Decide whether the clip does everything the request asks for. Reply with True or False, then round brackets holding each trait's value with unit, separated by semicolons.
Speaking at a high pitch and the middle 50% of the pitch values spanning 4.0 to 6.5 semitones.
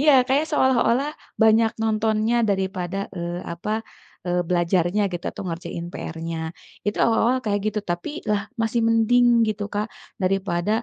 True (210 Hz; 4.4 semitones)